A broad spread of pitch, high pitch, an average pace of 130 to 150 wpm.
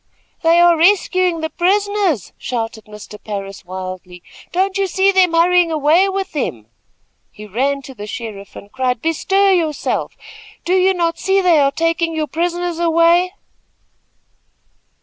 Yes: wide, 6.8 semitones; very high, 330 Hz; average, 145 wpm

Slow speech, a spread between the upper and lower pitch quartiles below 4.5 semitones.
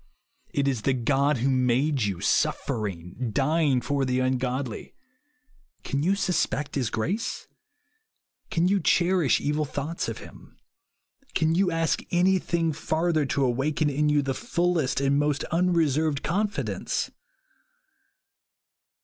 Yes: slow, 130 wpm; average, 4.1 semitones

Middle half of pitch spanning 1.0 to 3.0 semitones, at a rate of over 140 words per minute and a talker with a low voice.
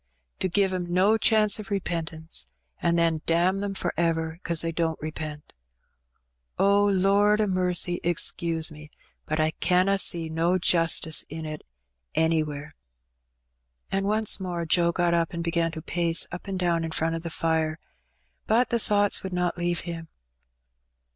No: average, 2.7 semitones; average, 160 wpm; medium, 170 Hz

